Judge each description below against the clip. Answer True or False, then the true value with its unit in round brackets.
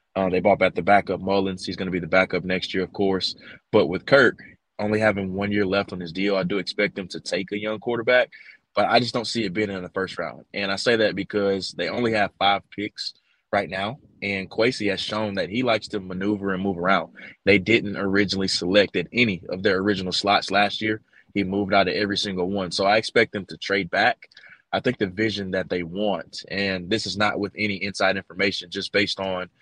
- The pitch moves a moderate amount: False (1.5 semitones)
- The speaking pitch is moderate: False (100 Hz)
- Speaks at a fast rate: True (235 wpm)